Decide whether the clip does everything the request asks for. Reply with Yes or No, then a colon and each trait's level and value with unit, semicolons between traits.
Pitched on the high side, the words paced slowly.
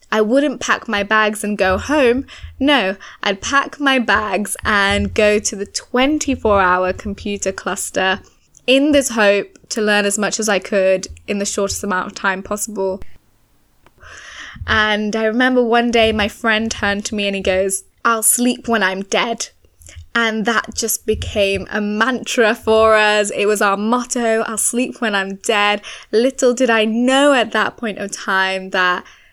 No: high, 215 Hz; average, 170 wpm